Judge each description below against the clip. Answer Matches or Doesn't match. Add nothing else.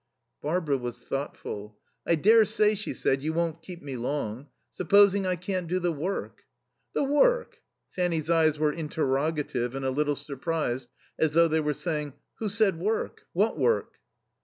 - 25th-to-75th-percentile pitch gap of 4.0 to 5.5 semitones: Matches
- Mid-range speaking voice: Matches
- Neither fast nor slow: Matches